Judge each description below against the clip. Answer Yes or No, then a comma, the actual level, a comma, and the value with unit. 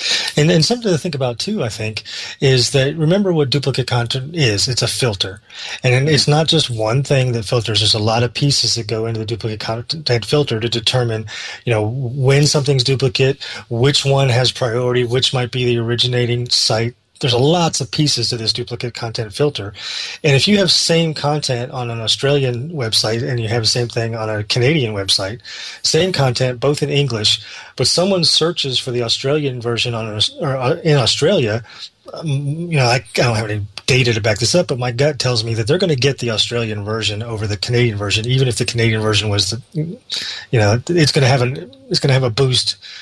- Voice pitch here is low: Yes, low, 125 Hz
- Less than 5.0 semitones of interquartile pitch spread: Yes, average, 3.8 semitones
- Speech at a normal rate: No, fast, 210 wpm